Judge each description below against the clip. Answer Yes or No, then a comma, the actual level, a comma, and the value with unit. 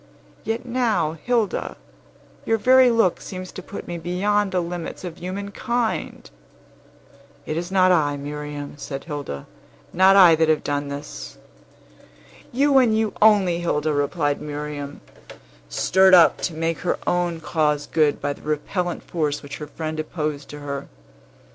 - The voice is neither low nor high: Yes, medium, 165 Hz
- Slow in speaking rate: No, average, 150 wpm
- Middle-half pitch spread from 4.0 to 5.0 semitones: Yes, average, 4.6 semitones